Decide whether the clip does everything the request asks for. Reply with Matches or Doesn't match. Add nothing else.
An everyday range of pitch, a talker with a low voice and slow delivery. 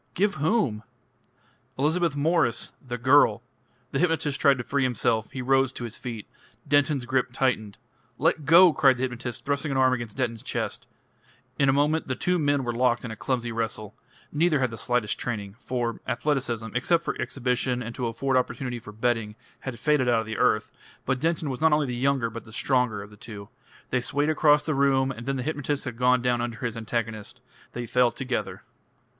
Doesn't match